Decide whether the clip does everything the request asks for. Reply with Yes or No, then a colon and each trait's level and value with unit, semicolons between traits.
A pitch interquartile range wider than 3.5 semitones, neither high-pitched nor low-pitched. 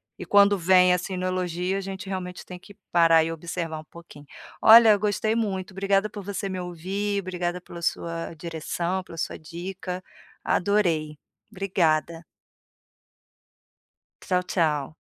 No: narrow, 2.6 semitones; medium, 180 Hz